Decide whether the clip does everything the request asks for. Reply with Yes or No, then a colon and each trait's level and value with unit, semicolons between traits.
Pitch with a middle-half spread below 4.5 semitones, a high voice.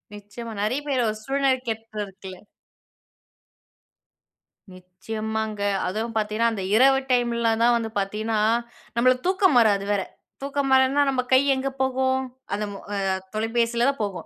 Yes: average, 3.7 semitones; high, 230 Hz